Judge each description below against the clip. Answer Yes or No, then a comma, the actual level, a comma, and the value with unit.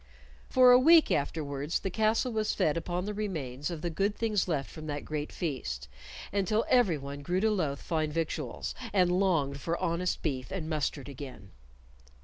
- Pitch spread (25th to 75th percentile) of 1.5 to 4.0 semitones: No, wide, 5.6 semitones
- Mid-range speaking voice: Yes, medium, 165 Hz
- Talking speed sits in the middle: Yes, average, 170 wpm